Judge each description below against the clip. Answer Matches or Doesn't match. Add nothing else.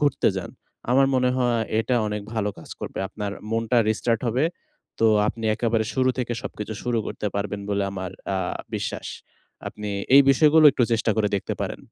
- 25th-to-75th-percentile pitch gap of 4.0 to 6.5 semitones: Doesn't match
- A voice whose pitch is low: Matches